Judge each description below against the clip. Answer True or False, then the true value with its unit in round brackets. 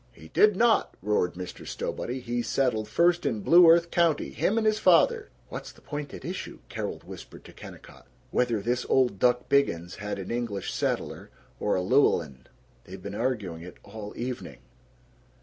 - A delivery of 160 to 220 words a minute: True (170 wpm)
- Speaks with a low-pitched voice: True (120 Hz)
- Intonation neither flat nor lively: False (7.1 semitones)